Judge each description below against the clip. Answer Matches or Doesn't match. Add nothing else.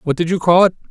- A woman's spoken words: Doesn't match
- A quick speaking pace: Matches